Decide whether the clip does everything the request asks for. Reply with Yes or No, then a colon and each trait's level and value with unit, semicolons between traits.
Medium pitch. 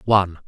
No: very low, 95 Hz